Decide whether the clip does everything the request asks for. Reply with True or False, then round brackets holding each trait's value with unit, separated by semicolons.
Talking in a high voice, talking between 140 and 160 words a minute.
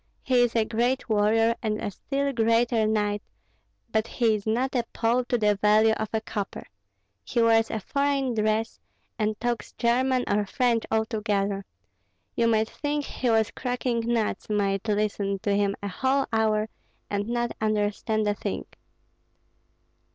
True (220 Hz; 155 wpm)